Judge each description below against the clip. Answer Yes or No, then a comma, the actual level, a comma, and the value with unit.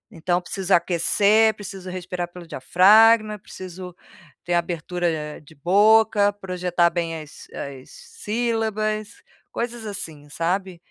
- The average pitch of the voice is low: No, medium, 185 Hz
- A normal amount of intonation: Yes, average, 3.6 semitones